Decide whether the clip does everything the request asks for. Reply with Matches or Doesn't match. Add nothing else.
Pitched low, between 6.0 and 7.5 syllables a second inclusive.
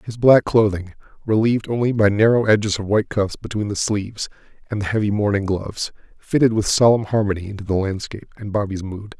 Matches